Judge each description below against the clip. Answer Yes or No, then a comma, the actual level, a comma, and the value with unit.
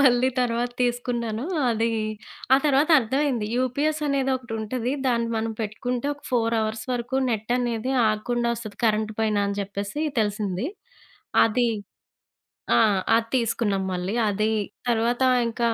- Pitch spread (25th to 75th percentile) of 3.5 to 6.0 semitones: No, narrow, 2.4 semitones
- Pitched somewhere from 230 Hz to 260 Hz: Yes, high, 235 Hz